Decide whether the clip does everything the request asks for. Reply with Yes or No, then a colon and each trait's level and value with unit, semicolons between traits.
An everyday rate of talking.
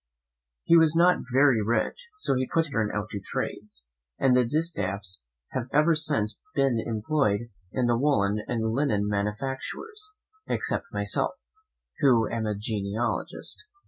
Yes: average, 145 wpm